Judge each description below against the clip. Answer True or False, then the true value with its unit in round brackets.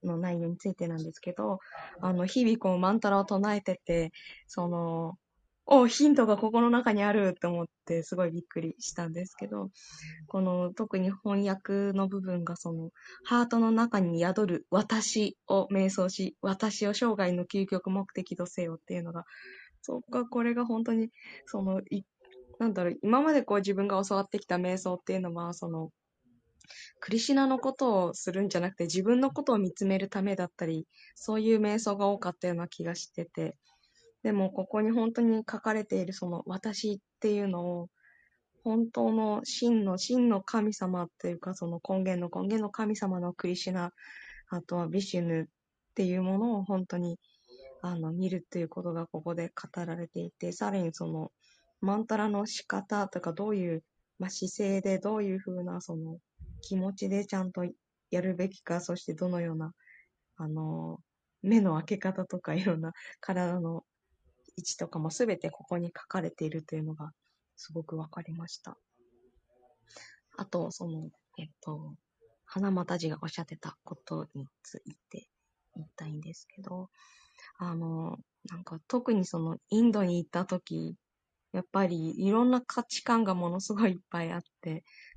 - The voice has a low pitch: False (185 Hz)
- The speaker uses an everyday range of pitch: True (3.4 semitones)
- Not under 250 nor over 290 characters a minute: False (325 characters per minute)